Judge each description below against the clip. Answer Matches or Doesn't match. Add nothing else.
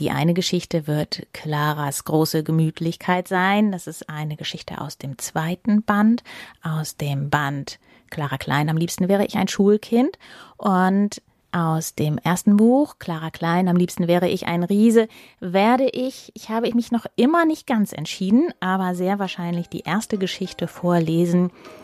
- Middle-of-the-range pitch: Matches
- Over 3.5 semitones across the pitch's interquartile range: Matches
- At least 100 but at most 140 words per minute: Doesn't match